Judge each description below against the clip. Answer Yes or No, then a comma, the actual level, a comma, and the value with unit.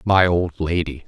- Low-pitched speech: Yes, very low, 85 Hz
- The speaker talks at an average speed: Yes, average, 165 wpm